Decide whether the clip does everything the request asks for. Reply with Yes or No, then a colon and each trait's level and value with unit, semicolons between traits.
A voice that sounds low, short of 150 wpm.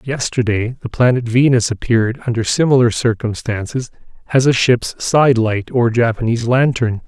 Yes: low, 120 Hz; slow, 135 wpm